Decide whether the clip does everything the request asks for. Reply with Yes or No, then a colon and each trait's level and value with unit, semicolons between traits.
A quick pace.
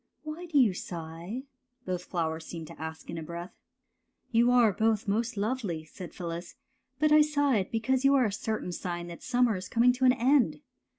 Yes: fast, 215 wpm